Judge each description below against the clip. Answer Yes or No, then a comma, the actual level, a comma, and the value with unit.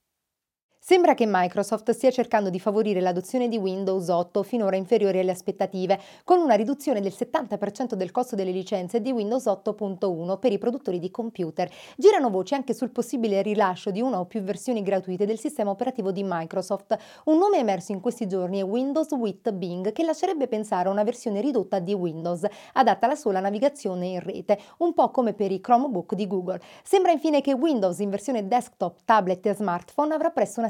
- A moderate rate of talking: No, fast, 185 wpm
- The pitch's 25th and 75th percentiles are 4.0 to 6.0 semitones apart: Yes, average, 4.6 semitones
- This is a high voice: Yes, high, 210 Hz